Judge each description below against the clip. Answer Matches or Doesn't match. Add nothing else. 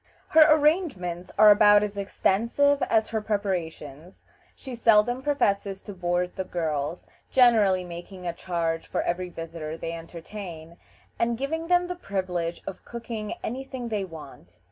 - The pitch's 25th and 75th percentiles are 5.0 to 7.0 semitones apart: Matches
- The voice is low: Doesn't match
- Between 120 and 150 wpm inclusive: Matches